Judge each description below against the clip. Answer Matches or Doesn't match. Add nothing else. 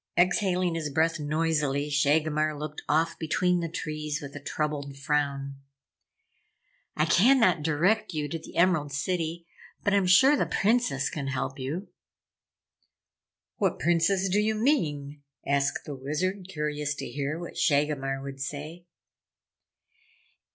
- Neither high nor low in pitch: Matches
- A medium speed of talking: Doesn't match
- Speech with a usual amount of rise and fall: Matches